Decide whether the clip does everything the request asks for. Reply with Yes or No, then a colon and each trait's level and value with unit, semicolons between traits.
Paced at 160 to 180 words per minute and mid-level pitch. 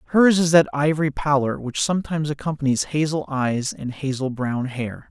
Yes: average, 165 wpm; medium, 145 Hz